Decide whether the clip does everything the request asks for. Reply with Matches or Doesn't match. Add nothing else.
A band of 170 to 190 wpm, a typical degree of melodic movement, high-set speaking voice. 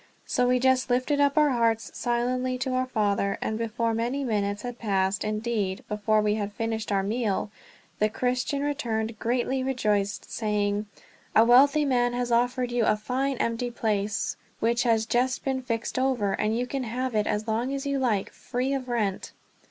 Matches